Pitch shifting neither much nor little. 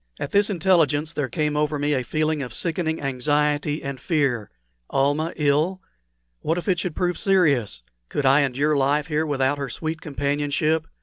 No: narrow, 2.3 semitones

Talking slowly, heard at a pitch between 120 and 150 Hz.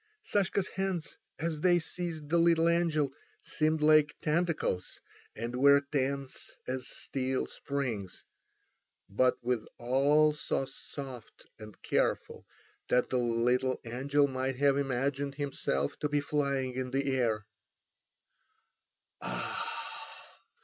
Yes: slow, 110 wpm; medium, 140 Hz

